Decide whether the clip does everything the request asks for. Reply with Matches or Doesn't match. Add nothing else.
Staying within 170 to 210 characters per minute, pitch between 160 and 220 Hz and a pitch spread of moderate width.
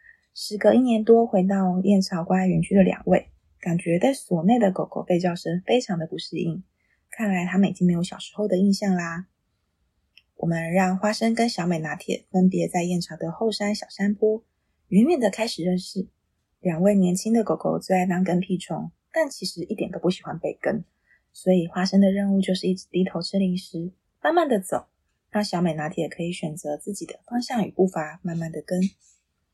Doesn't match